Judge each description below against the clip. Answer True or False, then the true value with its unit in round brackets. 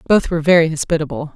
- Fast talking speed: False (180 wpm)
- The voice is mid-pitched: True (160 Hz)